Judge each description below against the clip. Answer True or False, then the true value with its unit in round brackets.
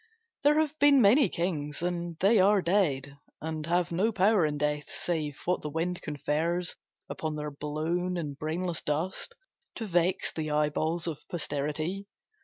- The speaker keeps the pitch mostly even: False (3.5 semitones)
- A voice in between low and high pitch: True (170 Hz)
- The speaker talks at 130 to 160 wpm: True (155 wpm)